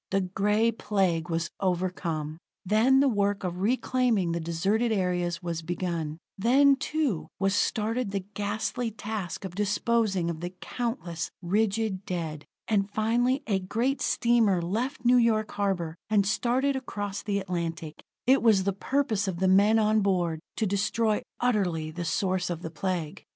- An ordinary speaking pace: Yes, average, 155 wpm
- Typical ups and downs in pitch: Yes, average, 4.3 semitones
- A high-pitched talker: Yes, high, 200 Hz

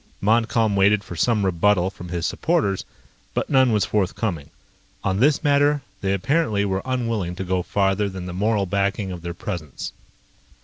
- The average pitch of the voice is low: Yes, low, 100 Hz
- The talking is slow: No, average, 165 wpm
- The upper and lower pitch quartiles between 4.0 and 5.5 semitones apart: No, average, 3.4 semitones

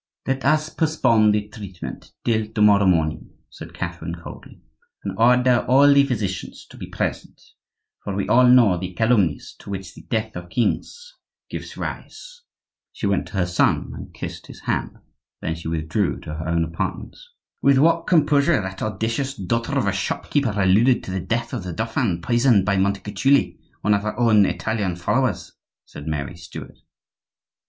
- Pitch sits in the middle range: No, low, 105 Hz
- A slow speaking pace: No, average, 170 wpm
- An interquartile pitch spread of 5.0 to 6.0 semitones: Yes, wide, 5.4 semitones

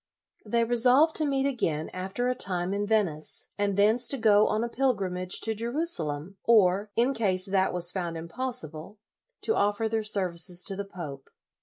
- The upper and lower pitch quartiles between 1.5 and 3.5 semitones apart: No, average, 4.6 semitones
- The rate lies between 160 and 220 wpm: Yes, average, 170 wpm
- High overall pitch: Yes, high, 205 Hz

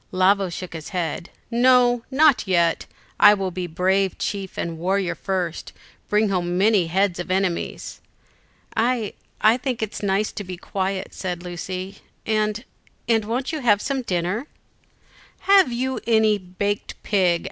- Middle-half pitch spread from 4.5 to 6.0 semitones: No, average, 3.6 semitones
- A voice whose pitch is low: No, high, 195 Hz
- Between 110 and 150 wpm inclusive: Yes, average, 145 wpm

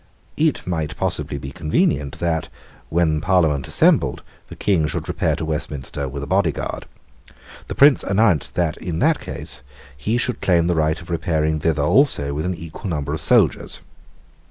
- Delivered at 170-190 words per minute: Yes, average, 175 wpm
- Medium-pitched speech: No, very low, 80 Hz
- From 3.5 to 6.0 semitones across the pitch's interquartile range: No, average, 3.1 semitones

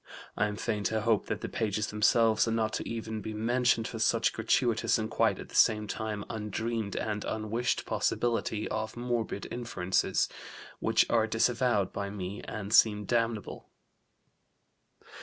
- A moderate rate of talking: Yes, average, 150 wpm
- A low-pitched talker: Yes, low, 110 Hz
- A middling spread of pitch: No, narrow, 1.5 semitones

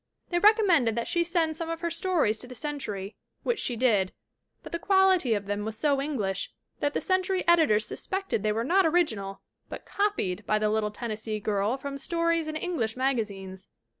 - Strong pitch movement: Yes, wide, 8.2 semitones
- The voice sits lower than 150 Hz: No, very high, 270 Hz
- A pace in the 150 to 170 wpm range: No, average, 195 wpm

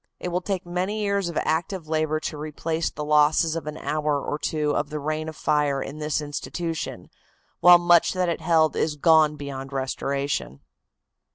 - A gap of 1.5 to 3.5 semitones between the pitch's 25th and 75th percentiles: Yes, narrow, 2.4 semitones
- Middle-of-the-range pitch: Yes, medium, 155 Hz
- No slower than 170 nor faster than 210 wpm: Yes, average, 180 wpm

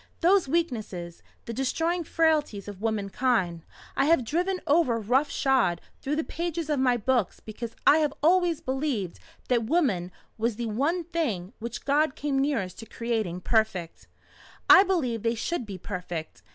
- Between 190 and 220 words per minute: No, average, 155 wpm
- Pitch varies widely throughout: Yes, wide, 6.7 semitones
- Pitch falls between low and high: No, very high, 255 Hz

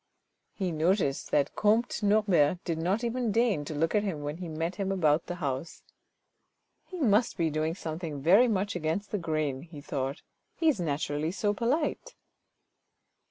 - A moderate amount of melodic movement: Yes, average, 5.0 semitones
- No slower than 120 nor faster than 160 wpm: No, average, 175 wpm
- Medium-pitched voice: Yes, medium, 175 Hz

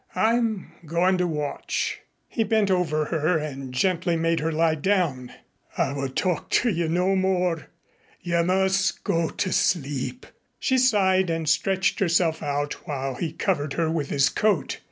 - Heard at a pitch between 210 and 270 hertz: No, medium, 170 Hz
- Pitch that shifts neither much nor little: Yes, average, 3.8 semitones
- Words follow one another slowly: No, average, 155 wpm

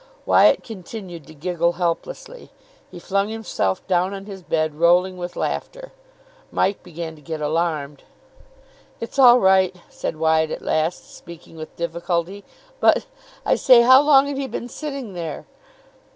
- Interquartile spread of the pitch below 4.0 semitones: No, wide, 5.4 semitones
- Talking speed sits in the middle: Yes, average, 150 wpm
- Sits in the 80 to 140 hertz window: No, medium, 180 Hz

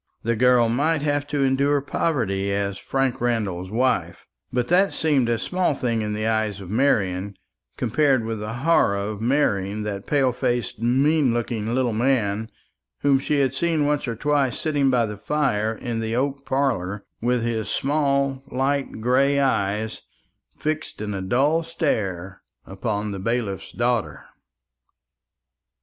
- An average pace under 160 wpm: Yes, average, 150 wpm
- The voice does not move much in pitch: No, average, 4.7 semitones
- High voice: No, low, 120 Hz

